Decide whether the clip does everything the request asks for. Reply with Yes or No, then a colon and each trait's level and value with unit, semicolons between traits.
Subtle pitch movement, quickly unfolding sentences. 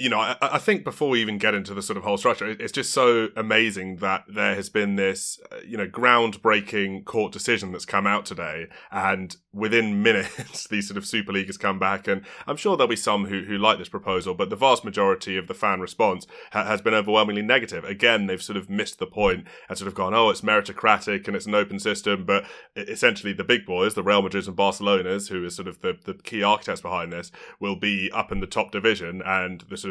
Yes: narrow, 1.7 semitones; fast, 235 wpm